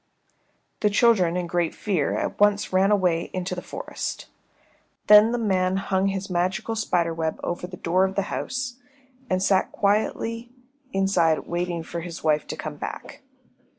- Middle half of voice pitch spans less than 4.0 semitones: Yes, average, 3.0 semitones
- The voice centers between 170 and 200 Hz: Yes, medium, 185 Hz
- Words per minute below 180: Yes, average, 160 wpm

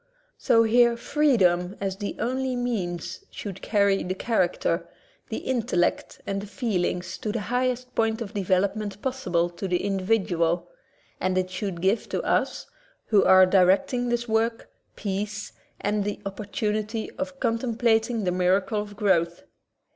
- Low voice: No, high, 205 Hz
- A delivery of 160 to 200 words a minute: No, average, 145 wpm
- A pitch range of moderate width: Yes, average, 3.7 semitones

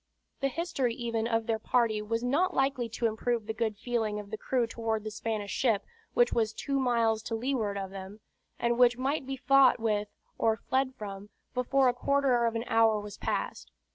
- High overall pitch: Yes, high, 230 Hz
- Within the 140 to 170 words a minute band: No, average, 200 wpm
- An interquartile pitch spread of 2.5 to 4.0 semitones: Yes, average, 2.8 semitones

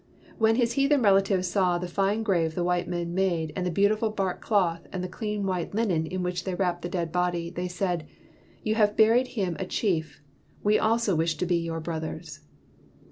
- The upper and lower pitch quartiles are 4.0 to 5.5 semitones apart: No, average, 3.3 semitones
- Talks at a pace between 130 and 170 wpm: No, average, 200 wpm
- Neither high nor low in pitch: Yes, medium, 180 Hz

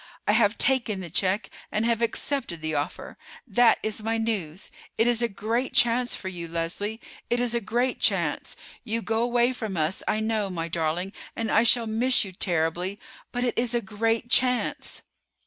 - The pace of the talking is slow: No, average, 185 wpm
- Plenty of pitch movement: No, average, 4.0 semitones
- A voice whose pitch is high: Yes, high, 220 Hz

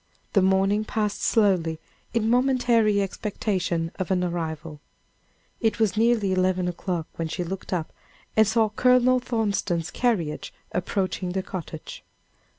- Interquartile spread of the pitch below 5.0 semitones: Yes, average, 4.0 semitones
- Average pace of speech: No, slow, 130 wpm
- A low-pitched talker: No, high, 195 Hz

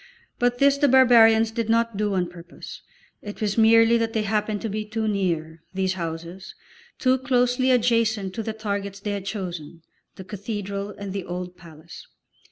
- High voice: Yes, high, 210 Hz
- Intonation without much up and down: No, average, 3.3 semitones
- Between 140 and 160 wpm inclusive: No, average, 175 wpm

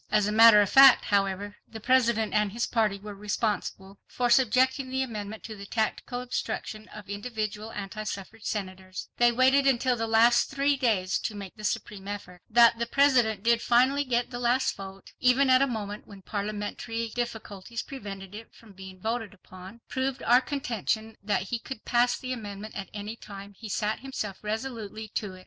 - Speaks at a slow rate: No, average, 185 wpm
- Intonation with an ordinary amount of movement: Yes, average, 3.2 semitones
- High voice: Yes, high, 220 Hz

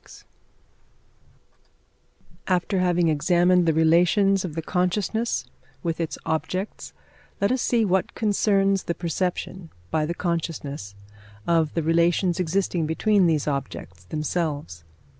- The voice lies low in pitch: No, medium, 175 Hz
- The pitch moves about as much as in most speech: Yes, average, 3.0 semitones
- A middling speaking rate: No, slow, 115 wpm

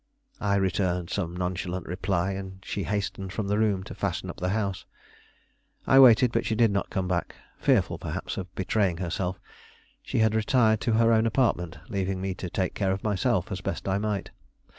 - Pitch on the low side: Yes, very low, 95 Hz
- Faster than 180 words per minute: Yes, average, 190 wpm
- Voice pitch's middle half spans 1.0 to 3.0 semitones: Yes, average, 2.7 semitones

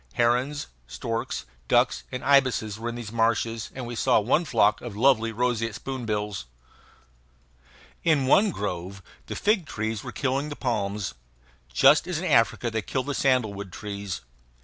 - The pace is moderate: Yes, average, 150 wpm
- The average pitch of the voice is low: Yes, low, 115 Hz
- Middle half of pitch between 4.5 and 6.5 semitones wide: No, average, 4.0 semitones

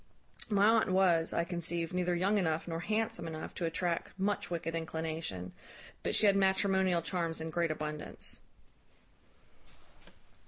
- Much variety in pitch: No, average, 2.8 semitones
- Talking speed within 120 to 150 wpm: Yes, slow, 135 wpm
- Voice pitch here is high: No, medium, 170 Hz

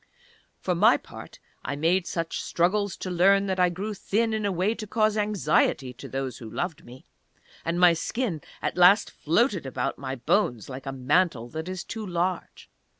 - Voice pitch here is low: No, medium, 175 Hz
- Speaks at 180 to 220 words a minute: Yes, average, 185 wpm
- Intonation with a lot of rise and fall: Yes, wide, 5.9 semitones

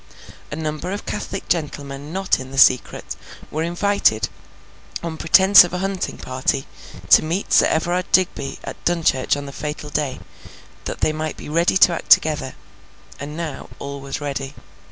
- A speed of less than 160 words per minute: No, average, 165 wpm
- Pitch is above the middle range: No, medium, 155 Hz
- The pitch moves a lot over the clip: No, average, 3.8 semitones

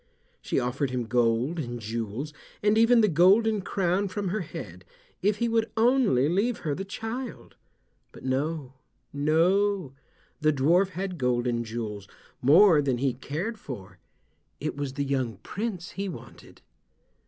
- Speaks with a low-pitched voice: No, medium, 155 Hz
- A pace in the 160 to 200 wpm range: No, average, 140 wpm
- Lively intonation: Yes, wide, 7.9 semitones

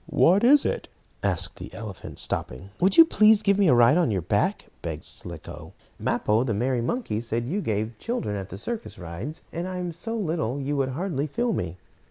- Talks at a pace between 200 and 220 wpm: Yes, fast, 205 wpm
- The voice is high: No, medium, 140 Hz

